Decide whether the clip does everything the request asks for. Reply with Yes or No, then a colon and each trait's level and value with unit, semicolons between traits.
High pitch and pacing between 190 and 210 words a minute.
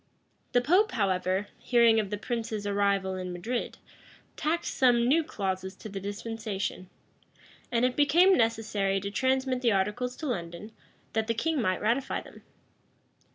No: high, 225 Hz; average, 150 wpm